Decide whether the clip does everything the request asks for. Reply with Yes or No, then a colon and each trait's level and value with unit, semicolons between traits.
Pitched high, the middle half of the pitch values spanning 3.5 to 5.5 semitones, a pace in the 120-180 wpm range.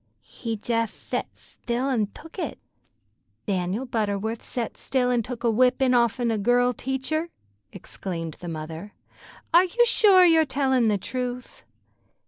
Yes: high, 245 Hz; average, 3.9 semitones; average, 140 wpm